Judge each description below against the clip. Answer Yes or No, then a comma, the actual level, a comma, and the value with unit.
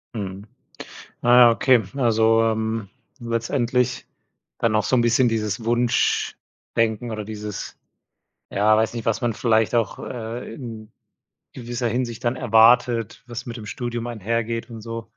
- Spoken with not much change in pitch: Yes, narrow, 1.4 semitones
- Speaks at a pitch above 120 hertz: No, low, 115 Hz